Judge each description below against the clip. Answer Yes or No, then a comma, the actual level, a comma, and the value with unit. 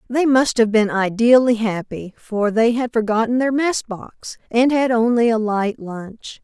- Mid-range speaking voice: No, high, 230 Hz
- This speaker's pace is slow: No, average, 175 wpm